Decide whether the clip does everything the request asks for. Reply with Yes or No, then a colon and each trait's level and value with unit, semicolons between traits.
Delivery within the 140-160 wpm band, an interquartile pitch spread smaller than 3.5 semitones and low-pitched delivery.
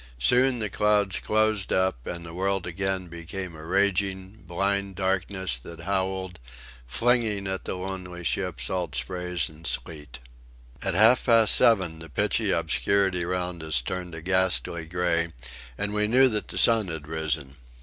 Yes: average, 155 wpm; average, 3.1 semitones; very low, 95 Hz